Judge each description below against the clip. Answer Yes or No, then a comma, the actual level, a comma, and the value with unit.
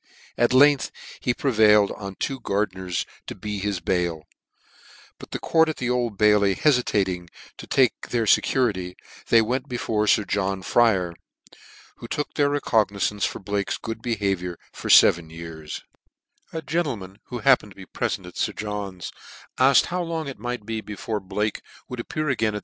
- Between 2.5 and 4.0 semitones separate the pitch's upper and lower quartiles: No, average, 4.4 semitones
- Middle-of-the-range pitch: No, low, 105 Hz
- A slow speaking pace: No, average, 170 wpm